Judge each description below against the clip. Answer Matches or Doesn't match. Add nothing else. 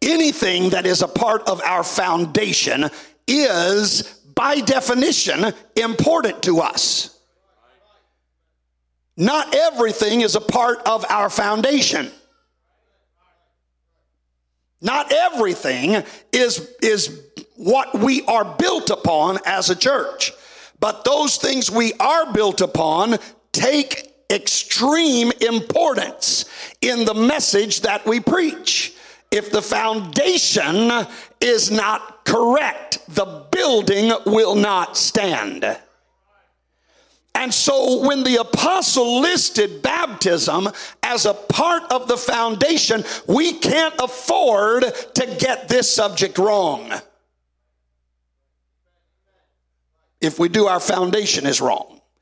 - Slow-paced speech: Matches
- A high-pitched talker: Matches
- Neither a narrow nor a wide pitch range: Doesn't match